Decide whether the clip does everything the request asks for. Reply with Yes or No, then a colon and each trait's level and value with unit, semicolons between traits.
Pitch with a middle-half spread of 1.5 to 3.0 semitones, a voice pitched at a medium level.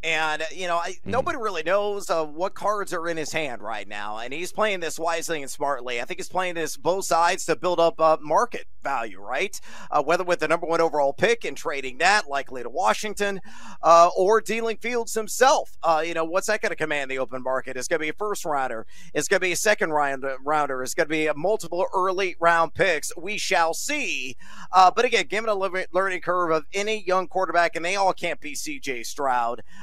No: average, 4.1 semitones; medium, 175 Hz